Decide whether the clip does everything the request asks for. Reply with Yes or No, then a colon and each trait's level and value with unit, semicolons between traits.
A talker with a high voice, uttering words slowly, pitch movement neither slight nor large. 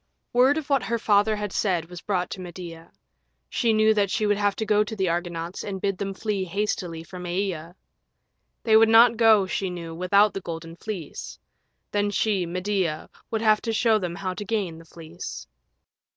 No: high, 195 Hz; average, 195 wpm; average, 3.6 semitones